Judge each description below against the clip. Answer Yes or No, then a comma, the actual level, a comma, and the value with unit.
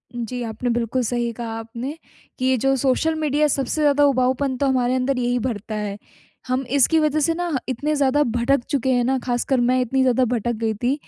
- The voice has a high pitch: Yes, very high, 255 Hz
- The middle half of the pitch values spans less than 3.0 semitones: Yes, narrow, 2.5 semitones